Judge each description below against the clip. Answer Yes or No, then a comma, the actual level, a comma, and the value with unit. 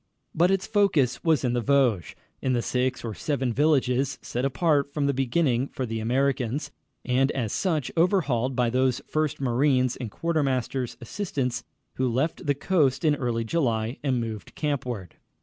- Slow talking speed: No, average, 165 wpm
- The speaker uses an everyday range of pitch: Yes, average, 3.3 semitones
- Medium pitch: No, low, 130 Hz